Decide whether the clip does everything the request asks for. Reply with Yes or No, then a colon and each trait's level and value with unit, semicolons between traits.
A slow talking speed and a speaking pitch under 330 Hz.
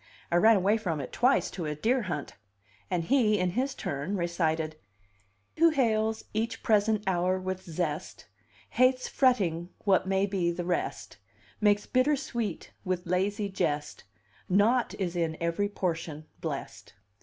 No: average, 145 wpm; high, 190 Hz